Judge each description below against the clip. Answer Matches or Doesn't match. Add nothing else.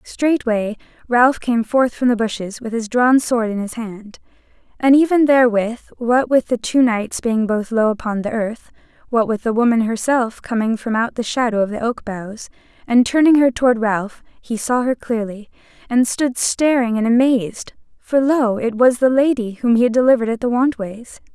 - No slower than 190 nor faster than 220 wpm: Matches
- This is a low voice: Doesn't match